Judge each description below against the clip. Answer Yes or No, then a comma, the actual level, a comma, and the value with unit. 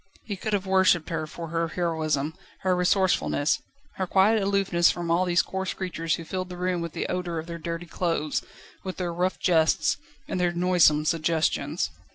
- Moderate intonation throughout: No, narrow, 2.0 semitones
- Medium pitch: Yes, medium, 175 Hz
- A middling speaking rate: Yes, average, 185 wpm